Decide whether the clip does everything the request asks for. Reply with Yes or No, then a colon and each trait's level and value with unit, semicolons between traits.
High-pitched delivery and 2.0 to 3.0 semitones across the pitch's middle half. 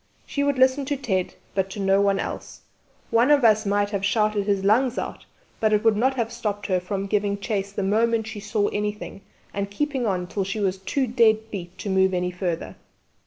Yes: high, 205 Hz; average, 2.7 semitones